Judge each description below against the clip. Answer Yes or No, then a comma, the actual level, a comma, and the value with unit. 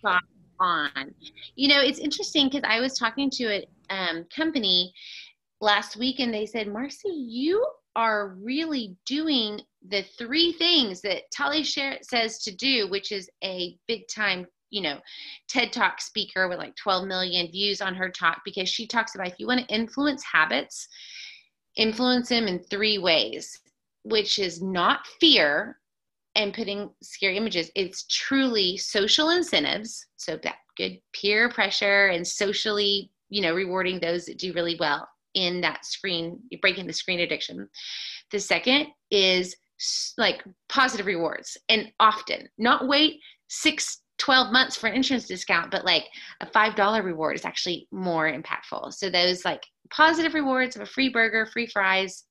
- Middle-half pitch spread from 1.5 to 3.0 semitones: No, wide, 5.6 semitones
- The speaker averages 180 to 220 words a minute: No, average, 155 wpm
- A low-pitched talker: No, high, 210 Hz